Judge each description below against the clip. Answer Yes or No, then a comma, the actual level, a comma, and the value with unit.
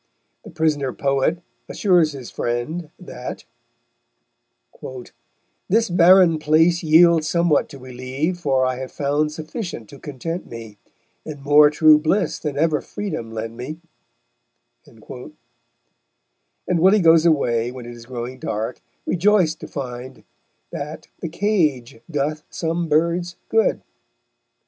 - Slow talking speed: Yes, slow, 120 wpm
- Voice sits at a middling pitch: Yes, medium, 150 Hz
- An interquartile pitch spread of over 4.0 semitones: Yes, average, 4.8 semitones